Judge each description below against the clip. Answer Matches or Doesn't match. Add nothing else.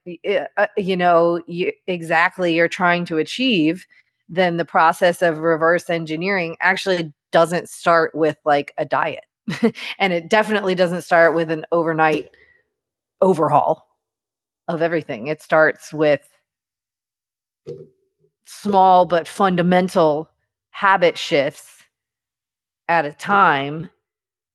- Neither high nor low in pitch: Matches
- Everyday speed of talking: Doesn't match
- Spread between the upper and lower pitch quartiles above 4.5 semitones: Doesn't match